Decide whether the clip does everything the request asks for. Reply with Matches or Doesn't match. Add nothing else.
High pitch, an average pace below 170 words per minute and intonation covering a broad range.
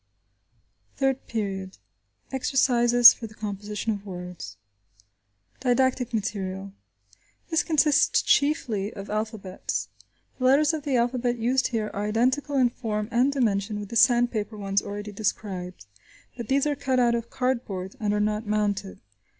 Doesn't match